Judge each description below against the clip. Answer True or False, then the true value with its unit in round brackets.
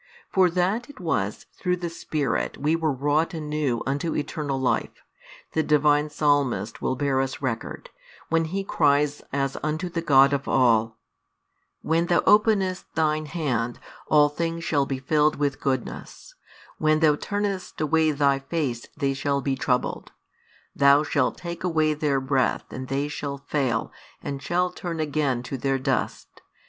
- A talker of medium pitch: True (145 Hz)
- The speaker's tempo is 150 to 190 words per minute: True (155 wpm)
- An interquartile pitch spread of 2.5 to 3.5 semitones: True (3.1 semitones)